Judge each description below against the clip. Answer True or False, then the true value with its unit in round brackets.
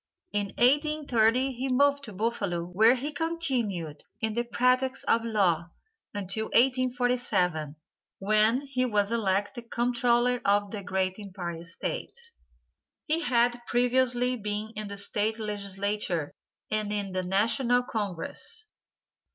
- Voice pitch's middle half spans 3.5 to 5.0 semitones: True (3.9 semitones)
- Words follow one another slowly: True (120 wpm)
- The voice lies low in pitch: False (220 Hz)